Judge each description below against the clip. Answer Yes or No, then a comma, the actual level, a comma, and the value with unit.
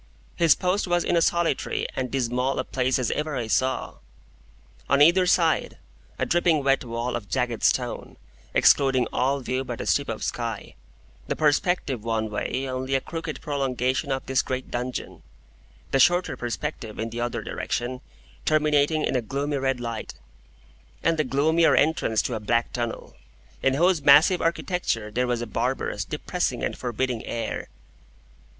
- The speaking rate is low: No, average, 160 wpm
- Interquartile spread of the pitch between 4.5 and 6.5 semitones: No, average, 4.1 semitones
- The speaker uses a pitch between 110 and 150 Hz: Yes, low, 135 Hz